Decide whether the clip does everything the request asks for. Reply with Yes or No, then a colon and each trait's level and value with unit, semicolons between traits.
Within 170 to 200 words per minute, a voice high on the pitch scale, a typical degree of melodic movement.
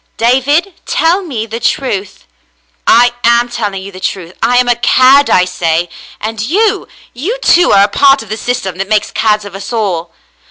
Yes: average, 195 wpm; high, 225 Hz; average, 4.9 semitones